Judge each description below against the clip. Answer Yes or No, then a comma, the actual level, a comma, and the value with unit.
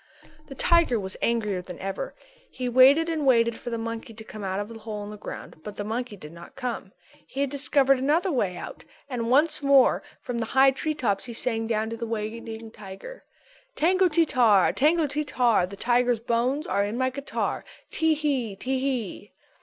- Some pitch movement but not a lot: Yes, average, 4.4 semitones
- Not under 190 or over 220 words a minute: Yes, fast, 205 wpm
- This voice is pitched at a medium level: No, high, 240 Hz